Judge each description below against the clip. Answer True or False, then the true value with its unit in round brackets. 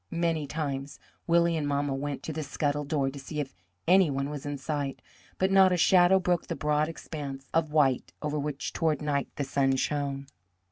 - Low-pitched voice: False (150 Hz)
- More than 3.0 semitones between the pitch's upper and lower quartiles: False (2.7 semitones)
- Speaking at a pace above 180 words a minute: True (195 wpm)